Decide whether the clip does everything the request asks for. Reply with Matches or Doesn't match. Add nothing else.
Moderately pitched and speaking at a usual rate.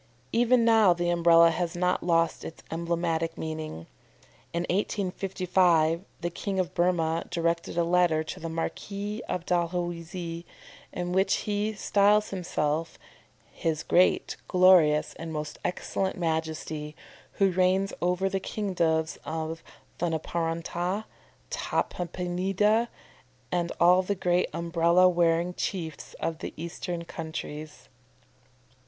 Doesn't match